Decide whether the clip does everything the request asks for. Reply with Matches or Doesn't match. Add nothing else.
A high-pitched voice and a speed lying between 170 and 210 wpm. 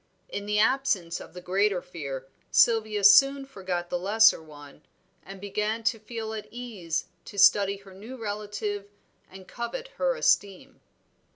Doesn't match